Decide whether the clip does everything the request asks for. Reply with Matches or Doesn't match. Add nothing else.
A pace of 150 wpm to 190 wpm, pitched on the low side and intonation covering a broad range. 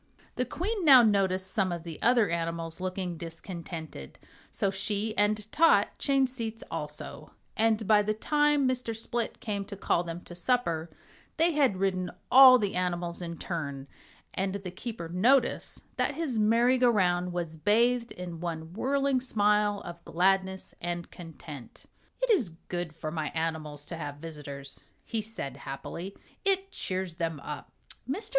Doesn't match